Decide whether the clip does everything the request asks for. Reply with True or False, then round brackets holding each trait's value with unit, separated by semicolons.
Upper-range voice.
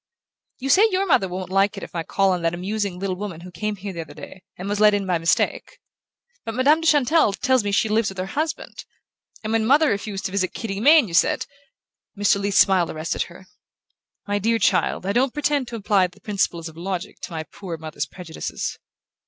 True (200 Hz)